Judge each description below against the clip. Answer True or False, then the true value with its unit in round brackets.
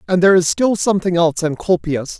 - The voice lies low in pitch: False (180 Hz)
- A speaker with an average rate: True (190 wpm)